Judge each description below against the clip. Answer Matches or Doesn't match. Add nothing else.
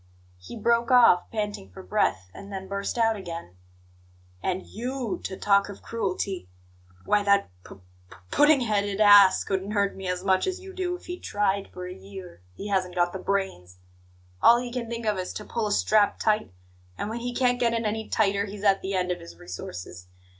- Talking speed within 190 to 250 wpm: Matches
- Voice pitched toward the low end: Doesn't match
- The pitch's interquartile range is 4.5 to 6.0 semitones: Doesn't match